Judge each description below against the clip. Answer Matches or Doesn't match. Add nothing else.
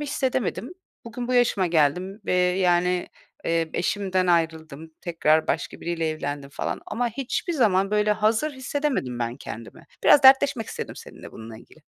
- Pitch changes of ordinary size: Doesn't match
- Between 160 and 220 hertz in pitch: Matches